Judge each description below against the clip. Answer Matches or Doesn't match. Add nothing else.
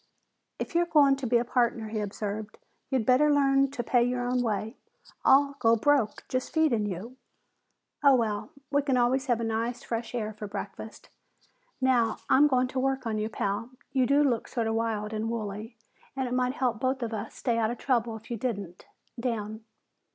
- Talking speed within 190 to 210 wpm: Matches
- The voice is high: Matches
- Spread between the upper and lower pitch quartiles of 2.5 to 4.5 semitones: Matches